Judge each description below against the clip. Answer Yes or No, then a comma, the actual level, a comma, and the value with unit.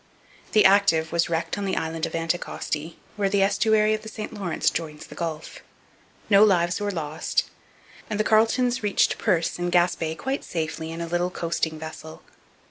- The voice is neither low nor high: Yes, medium, 175 Hz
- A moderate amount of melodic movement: Yes, average, 4.0 semitones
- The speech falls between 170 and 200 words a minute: Yes, average, 175 wpm